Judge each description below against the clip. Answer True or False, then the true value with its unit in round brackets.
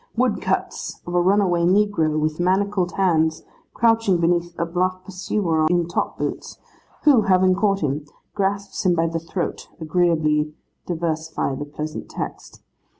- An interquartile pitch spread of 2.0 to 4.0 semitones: True (3.3 semitones)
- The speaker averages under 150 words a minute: True (140 wpm)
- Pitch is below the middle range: False (175 Hz)